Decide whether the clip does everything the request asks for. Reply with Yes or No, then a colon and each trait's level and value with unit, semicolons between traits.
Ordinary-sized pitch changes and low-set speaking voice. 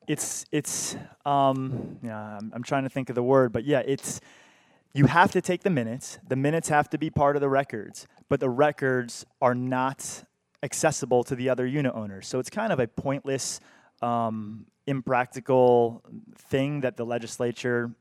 Yes: average, 3.0 semitones; low, 130 Hz